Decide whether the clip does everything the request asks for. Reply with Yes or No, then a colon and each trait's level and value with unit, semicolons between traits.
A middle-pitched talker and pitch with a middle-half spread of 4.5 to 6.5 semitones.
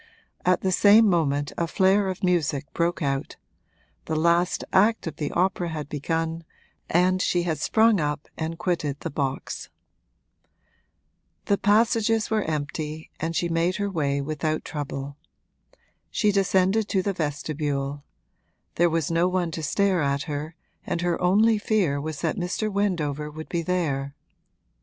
No: medium, 165 Hz; average, 4.0 semitones